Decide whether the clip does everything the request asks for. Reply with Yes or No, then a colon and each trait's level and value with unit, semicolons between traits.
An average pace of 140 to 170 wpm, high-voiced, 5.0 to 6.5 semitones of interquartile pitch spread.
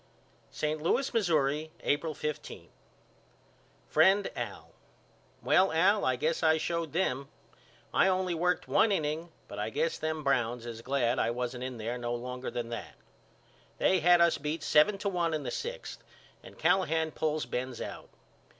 No: average, 160 wpm; medium, 155 Hz; wide, 5.6 semitones